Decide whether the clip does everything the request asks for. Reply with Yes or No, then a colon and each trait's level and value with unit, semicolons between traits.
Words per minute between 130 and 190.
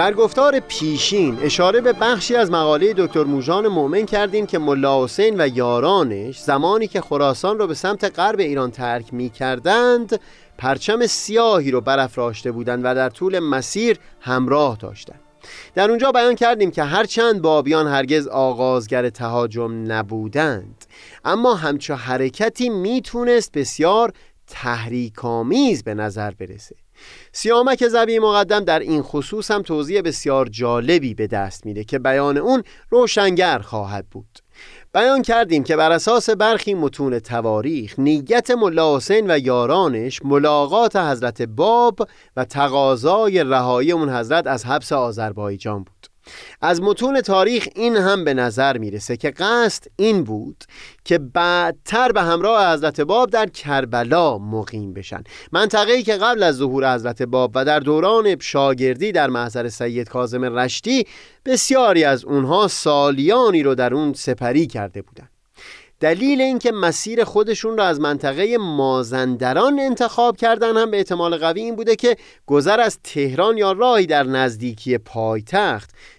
Yes: average, 140 wpm